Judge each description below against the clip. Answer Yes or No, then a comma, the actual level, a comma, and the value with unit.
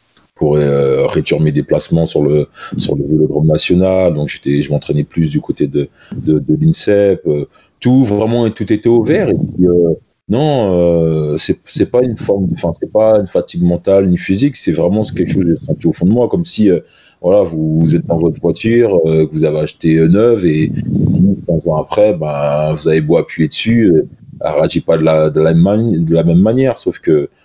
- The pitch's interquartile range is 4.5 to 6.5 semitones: Yes, wide, 5.4 semitones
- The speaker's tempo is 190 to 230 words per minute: Yes, fast, 220 wpm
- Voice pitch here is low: Yes, very low, 85 Hz